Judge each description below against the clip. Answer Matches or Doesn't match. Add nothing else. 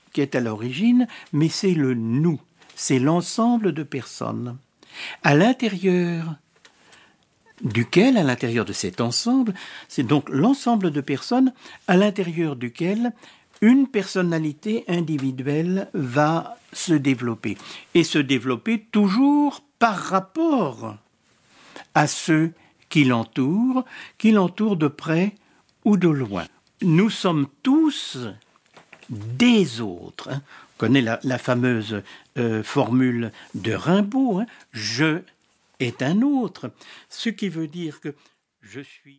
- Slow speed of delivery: Matches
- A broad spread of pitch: Matches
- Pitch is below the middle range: Doesn't match